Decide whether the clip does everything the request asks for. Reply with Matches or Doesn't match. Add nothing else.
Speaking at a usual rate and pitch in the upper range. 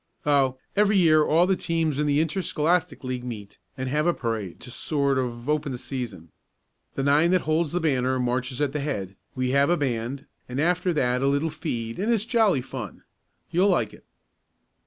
Doesn't match